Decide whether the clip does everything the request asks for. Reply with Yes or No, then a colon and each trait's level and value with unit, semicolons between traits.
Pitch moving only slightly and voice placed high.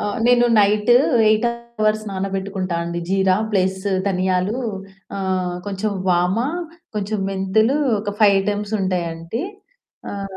Yes: narrow, 2.3 semitones; high, 195 Hz